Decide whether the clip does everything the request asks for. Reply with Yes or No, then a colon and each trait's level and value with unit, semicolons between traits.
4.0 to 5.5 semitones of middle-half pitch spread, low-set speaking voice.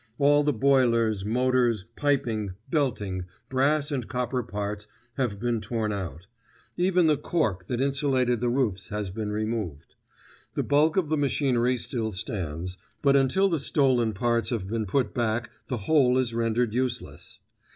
Yes: average, 4.4 semitones; low, 120 Hz